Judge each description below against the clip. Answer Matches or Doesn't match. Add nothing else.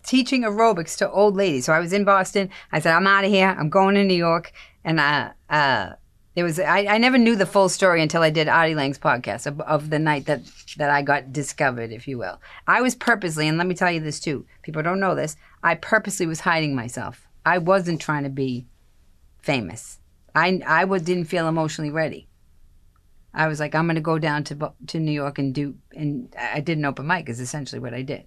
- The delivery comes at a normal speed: Doesn't match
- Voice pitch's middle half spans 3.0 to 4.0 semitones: Doesn't match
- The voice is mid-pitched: Matches